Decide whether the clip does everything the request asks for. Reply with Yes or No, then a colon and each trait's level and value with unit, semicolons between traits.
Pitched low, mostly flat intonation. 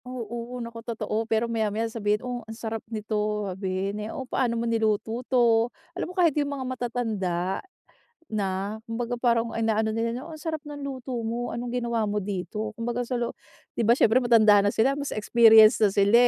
No: high, 230 Hz; narrow, 2.3 semitones